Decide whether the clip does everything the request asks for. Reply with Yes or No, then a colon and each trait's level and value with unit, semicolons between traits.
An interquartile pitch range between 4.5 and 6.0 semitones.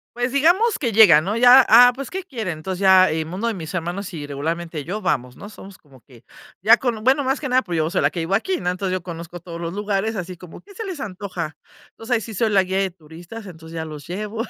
Yes: wide, 5.5 semitones